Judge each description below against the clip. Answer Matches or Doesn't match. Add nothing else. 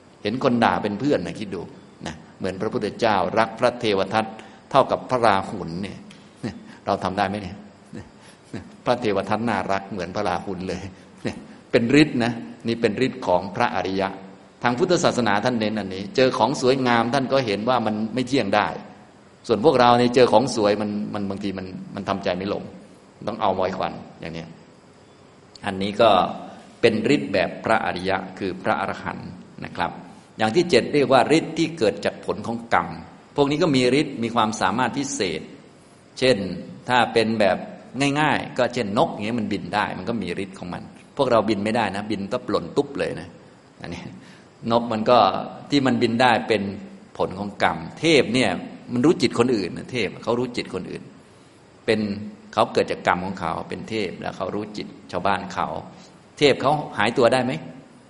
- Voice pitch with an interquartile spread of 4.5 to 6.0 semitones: Doesn't match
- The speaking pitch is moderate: Doesn't match